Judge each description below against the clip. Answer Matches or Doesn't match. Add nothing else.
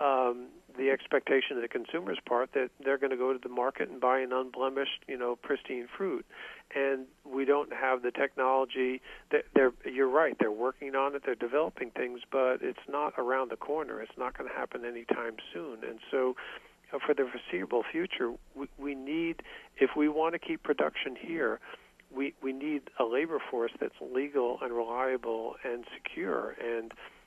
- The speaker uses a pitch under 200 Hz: Matches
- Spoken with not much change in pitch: Matches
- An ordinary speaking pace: Matches